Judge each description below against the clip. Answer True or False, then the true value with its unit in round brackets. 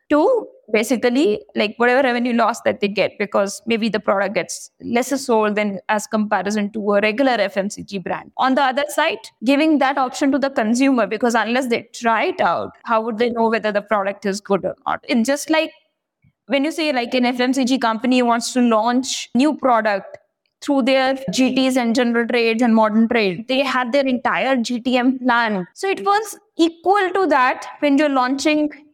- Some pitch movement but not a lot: True (4.1 semitones)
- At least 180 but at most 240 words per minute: True (185 wpm)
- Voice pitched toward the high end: True (245 Hz)